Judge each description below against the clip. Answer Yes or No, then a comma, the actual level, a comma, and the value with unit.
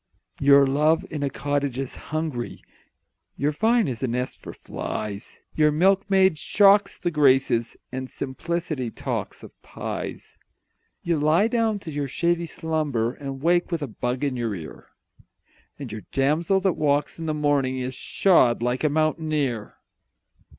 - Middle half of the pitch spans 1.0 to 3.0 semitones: No, average, 4.1 semitones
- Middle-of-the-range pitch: Yes, medium, 145 Hz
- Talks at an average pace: Yes, average, 150 wpm